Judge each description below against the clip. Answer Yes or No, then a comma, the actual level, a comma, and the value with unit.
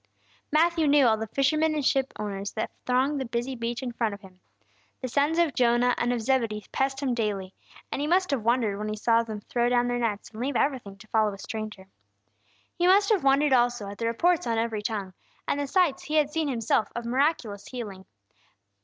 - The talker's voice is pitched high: Yes, high, 240 Hz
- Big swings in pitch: No, average, 4.5 semitones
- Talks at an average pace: No, fast, 215 wpm